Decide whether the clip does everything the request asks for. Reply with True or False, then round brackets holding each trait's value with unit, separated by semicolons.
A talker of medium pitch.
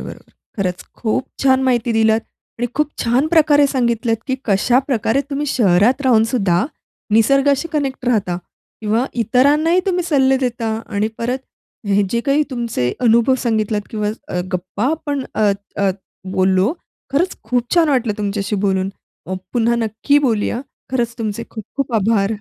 False (235 Hz)